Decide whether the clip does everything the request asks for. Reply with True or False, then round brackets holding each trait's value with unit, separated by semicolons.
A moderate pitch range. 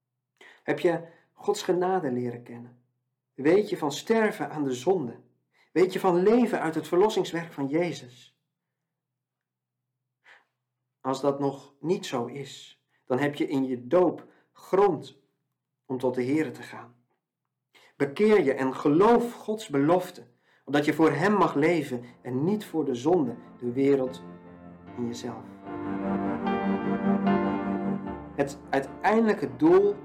False (5.9 semitones)